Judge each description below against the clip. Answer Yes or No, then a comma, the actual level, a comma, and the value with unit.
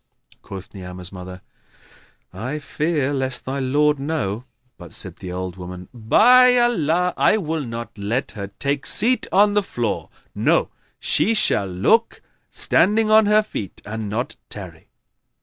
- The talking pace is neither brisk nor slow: Yes, average, 145 wpm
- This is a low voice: Yes, low, 130 Hz